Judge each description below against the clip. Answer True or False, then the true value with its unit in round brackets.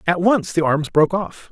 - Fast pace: True (235 wpm)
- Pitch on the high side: False (175 Hz)